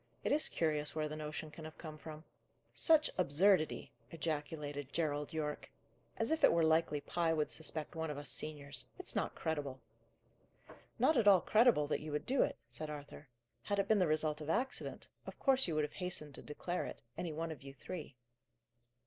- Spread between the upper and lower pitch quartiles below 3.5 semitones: Yes, average, 2.9 semitones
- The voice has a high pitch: No, medium, 155 Hz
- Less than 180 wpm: No, average, 195 wpm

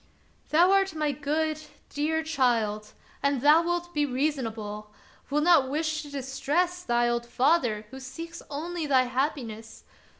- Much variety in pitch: No, average, 4.4 semitones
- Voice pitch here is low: No, very high, 285 Hz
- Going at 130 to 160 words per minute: Yes, average, 145 wpm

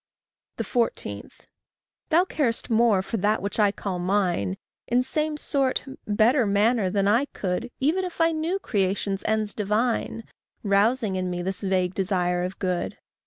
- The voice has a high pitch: Yes, high, 210 Hz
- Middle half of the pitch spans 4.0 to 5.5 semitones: Yes, average, 4.7 semitones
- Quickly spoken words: No, average, 150 wpm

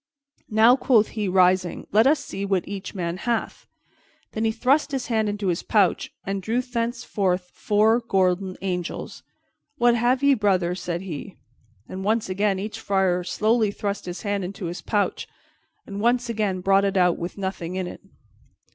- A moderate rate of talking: Yes, average, 170 wpm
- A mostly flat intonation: No, average, 3.3 semitones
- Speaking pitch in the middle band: No, high, 200 Hz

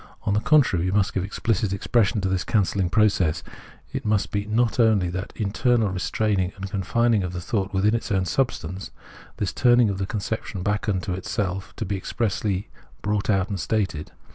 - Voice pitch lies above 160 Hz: No, low, 100 Hz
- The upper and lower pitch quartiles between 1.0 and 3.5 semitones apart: Yes, narrow, 2.5 semitones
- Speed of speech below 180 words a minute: No, average, 190 wpm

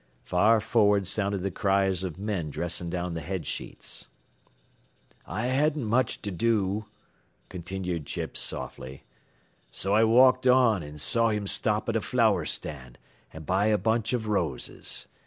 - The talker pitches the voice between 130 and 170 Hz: No, low, 100 Hz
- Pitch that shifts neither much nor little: Yes, average, 4.2 semitones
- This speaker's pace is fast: No, average, 150 wpm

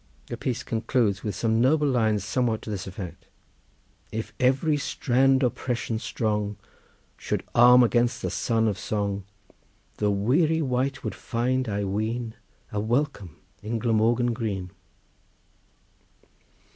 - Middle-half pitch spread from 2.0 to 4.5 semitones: Yes, average, 3.3 semitones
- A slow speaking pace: Yes, slow, 125 wpm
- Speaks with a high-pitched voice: No, low, 115 Hz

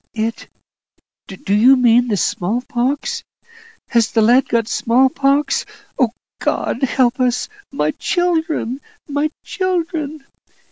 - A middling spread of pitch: Yes, average, 4.1 semitones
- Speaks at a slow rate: Yes, slow, 120 wpm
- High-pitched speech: Yes, very high, 255 Hz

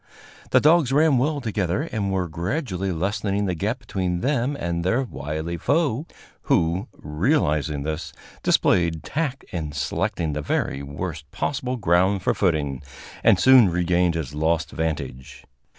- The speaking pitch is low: Yes, very low, 90 Hz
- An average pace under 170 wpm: Yes, average, 140 wpm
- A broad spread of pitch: Yes, wide, 7.4 semitones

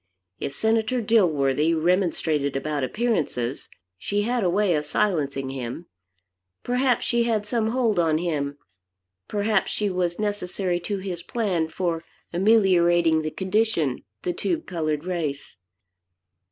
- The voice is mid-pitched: Yes, medium, 180 Hz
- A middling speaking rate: No, slow, 125 wpm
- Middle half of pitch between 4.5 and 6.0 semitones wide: Yes, average, 5.3 semitones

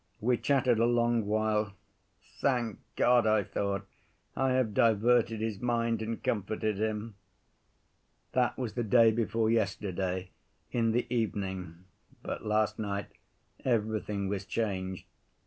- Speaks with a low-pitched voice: Yes, low, 110 Hz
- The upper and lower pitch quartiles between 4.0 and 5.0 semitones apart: No, narrow, 2.6 semitones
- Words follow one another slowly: Yes, slow, 125 wpm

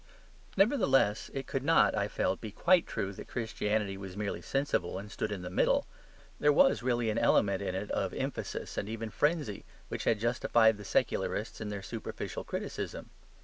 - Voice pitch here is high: No, low, 110 Hz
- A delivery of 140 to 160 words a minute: No, average, 180 wpm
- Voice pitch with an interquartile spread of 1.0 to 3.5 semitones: No, average, 4.7 semitones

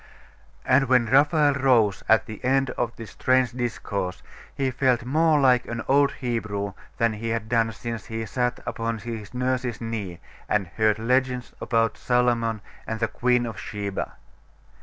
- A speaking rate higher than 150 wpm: Yes, average, 160 wpm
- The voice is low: Yes, low, 120 Hz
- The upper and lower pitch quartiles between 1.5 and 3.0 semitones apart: Yes, narrow, 2.4 semitones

